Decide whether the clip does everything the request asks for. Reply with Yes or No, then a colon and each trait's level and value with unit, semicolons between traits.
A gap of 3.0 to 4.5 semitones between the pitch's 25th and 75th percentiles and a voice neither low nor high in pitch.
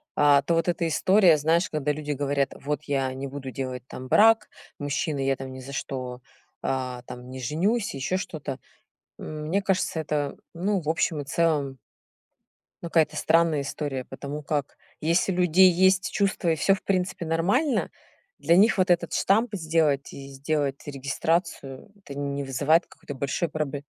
Yes: average, 3.8 semitones; medium, 150 Hz